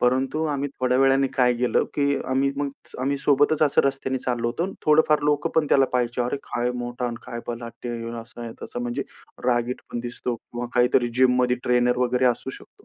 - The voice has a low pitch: Yes, low, 125 Hz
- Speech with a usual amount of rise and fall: No, narrow, 2.2 semitones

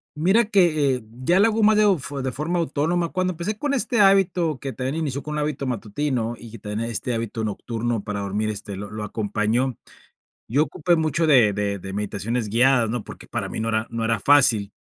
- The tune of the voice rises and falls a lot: Yes, wide, 6.8 semitones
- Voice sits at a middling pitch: No, low, 130 Hz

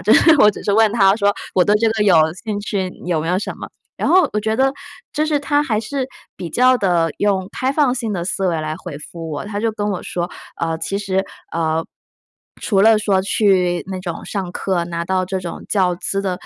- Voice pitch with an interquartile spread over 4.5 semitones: No, average, 3.7 semitones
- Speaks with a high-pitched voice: Yes, high, 195 Hz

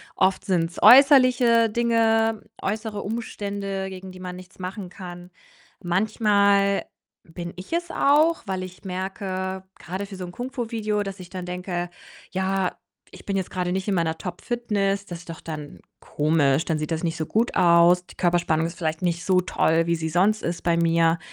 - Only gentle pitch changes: No, average, 3.0 semitones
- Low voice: No, medium, 185 Hz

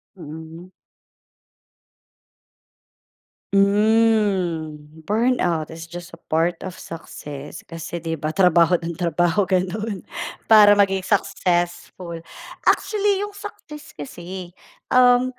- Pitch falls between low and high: Yes, medium, 180 Hz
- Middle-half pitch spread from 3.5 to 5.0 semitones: Yes, average, 4.2 semitones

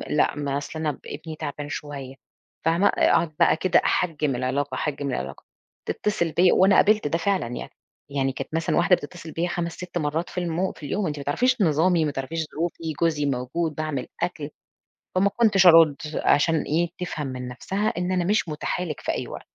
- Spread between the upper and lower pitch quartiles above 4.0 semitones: No, average, 3.6 semitones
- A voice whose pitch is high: No, medium, 160 Hz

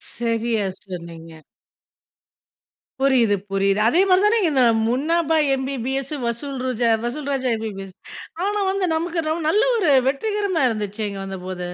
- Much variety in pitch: Yes, wide, 7.7 semitones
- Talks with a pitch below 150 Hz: No, very high, 255 Hz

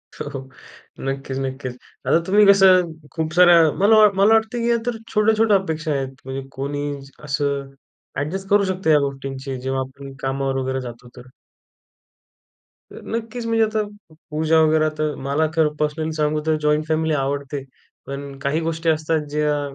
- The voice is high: No, medium, 150 Hz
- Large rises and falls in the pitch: No, average, 4.6 semitones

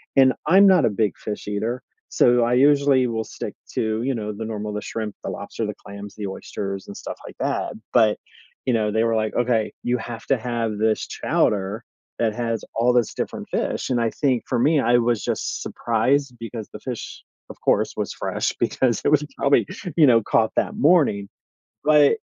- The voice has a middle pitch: No, low, 115 Hz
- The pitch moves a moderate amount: Yes, average, 3.0 semitones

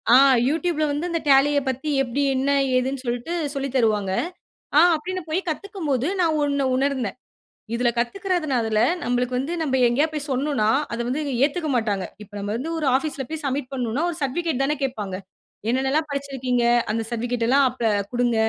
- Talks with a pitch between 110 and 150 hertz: No, very high, 270 Hz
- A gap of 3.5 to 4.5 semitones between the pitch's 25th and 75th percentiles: Yes, average, 3.8 semitones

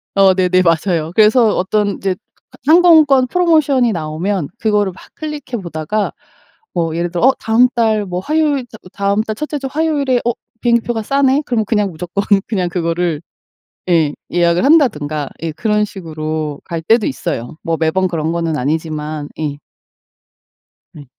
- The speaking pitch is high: Yes, high, 195 Hz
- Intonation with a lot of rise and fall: Yes, wide, 6.7 semitones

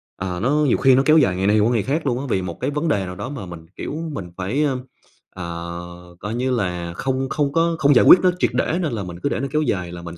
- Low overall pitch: Yes, low, 110 Hz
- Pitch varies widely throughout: Yes, wide, 8.0 semitones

